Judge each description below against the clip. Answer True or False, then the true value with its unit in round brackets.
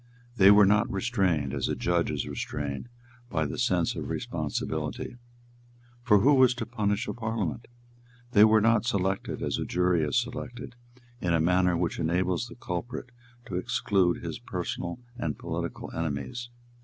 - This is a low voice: True (95 Hz)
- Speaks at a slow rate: False (155 wpm)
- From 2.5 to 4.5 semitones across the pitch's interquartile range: False (5.3 semitones)